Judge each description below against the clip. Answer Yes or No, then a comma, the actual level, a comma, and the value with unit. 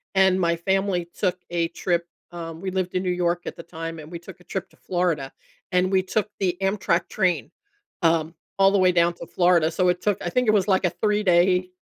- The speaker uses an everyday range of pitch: No, narrow, 2.0 semitones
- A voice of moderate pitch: Yes, medium, 180 Hz